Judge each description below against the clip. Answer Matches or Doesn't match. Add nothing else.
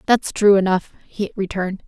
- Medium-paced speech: Matches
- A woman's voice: Matches